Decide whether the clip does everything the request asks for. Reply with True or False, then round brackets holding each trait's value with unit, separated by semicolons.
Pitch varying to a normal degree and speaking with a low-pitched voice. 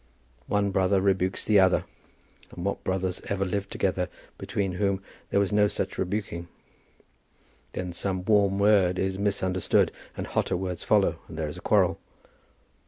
False (1.5 semitones; 95 Hz)